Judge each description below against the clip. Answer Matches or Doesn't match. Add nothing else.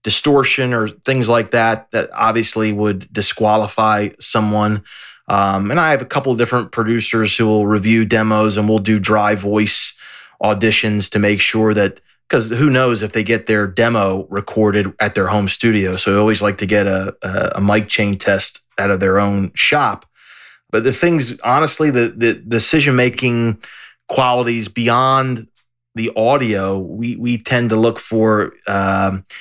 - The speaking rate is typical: Matches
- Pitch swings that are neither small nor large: Doesn't match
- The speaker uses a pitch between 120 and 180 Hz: Doesn't match